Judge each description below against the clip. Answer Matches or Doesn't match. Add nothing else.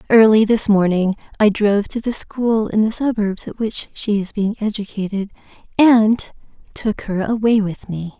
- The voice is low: Doesn't match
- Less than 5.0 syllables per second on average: Matches